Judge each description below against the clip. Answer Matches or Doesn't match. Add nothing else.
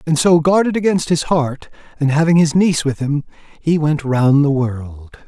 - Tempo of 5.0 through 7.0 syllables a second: Doesn't match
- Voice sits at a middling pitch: Matches